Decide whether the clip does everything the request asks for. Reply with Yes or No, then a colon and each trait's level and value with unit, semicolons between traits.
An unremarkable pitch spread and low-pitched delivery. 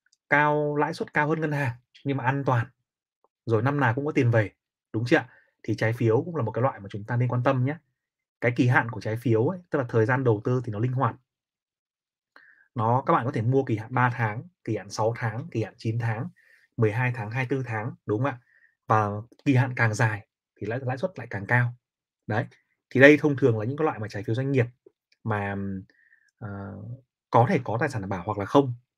Yes: average, 3.9 semitones; low, 125 Hz